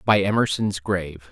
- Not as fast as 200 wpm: Yes, slow, 135 wpm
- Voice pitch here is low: Yes, very low, 95 Hz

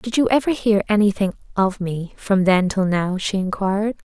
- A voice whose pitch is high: Yes, high, 200 Hz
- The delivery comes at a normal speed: Yes, average, 190 wpm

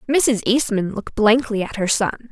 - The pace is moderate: Yes, average, 180 wpm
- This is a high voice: Yes, high, 225 Hz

